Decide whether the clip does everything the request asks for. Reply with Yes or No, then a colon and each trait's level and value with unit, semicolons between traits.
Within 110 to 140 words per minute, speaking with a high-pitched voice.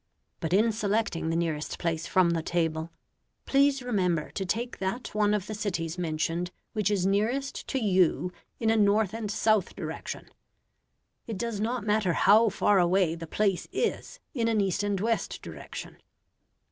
No: average, 165 wpm; high, 200 Hz